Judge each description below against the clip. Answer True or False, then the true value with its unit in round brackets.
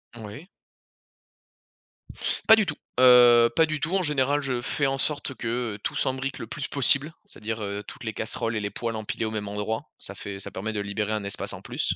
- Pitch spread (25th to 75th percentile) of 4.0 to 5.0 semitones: True (4.4 semitones)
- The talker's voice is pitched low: True (120 Hz)